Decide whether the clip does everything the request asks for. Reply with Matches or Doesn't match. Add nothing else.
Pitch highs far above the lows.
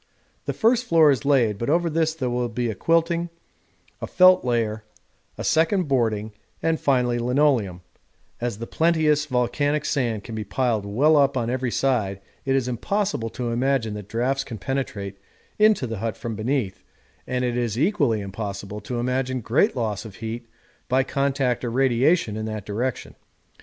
Doesn't match